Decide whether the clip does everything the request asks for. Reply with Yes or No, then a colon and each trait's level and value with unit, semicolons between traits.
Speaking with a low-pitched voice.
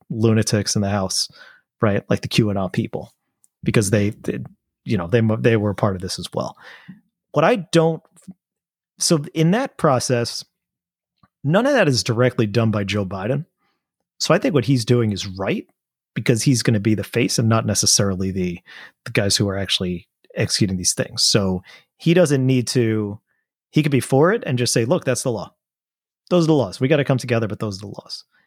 Yes: low, 120 Hz